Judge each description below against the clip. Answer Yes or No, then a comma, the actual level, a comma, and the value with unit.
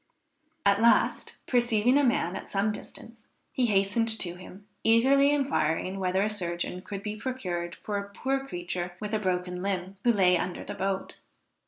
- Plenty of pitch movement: No, average, 4.1 semitones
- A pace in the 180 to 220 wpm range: No, average, 170 wpm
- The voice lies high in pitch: Yes, high, 200 Hz